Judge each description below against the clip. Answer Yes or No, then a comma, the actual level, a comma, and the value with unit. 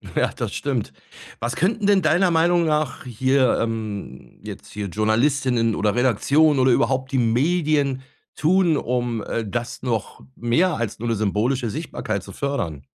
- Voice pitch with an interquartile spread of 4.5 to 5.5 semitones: Yes, average, 5.1 semitones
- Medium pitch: No, low, 125 Hz